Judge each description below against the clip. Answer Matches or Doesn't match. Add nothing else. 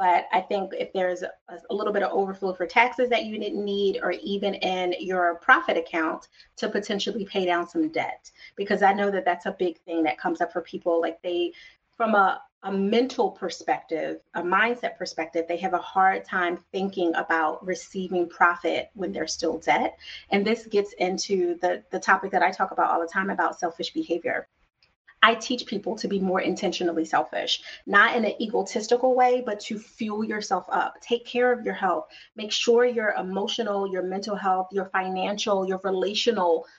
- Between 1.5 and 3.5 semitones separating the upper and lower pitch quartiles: Matches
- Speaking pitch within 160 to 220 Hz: Matches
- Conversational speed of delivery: Matches